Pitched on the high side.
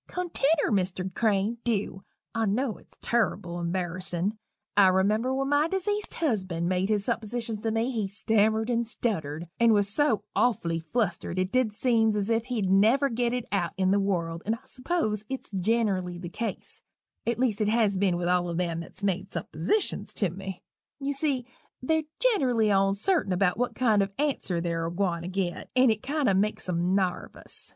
Yes: high, 210 Hz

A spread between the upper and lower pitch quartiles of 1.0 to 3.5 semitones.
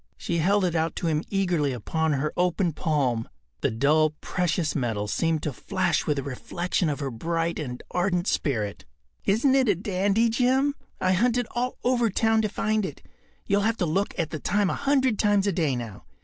No: wide, 5.4 semitones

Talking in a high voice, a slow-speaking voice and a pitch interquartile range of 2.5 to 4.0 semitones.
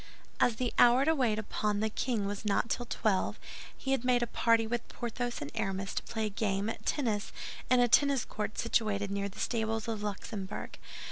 No: high, 220 Hz; fast, 205 wpm; average, 2.8 semitones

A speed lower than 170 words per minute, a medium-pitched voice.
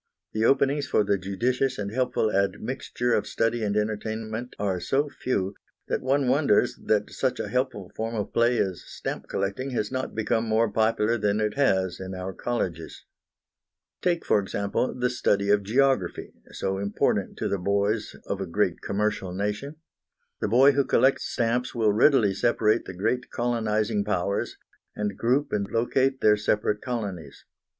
No: average, 160 wpm; low, 110 Hz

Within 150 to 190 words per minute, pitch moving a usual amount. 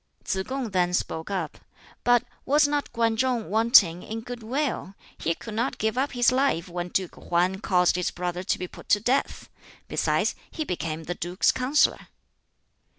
No: average, 175 wpm; wide, 5.8 semitones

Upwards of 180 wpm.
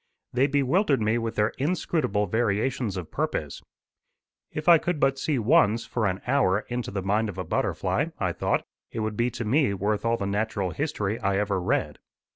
Yes: average, 190 wpm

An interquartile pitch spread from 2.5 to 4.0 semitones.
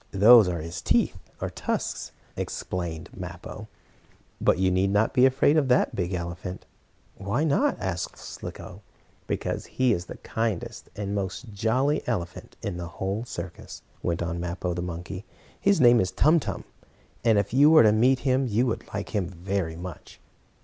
No: wide, 5.6 semitones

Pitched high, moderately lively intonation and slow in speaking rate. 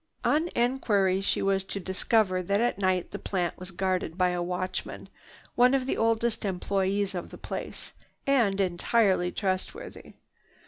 No: high, 195 Hz; average, 3.6 semitones; average, 150 wpm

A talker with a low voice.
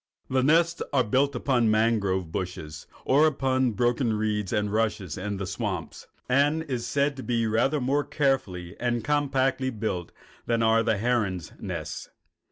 Yes: low, 120 Hz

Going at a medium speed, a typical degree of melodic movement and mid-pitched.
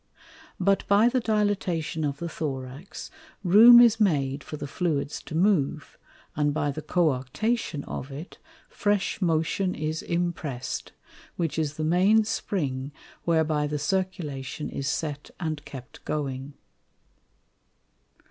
No: slow, 125 wpm; average, 4.7 semitones; medium, 155 Hz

